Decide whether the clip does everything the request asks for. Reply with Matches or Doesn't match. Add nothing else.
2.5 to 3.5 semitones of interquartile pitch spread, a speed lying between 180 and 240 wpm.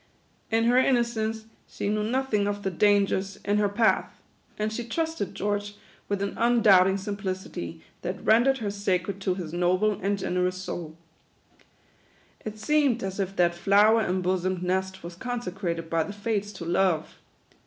Doesn't match